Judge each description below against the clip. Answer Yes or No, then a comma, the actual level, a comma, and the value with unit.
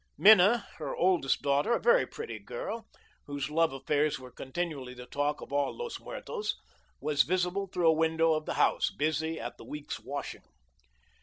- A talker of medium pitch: Yes, medium, 160 Hz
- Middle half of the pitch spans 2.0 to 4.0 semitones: No, average, 5.3 semitones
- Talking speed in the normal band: Yes, average, 170 wpm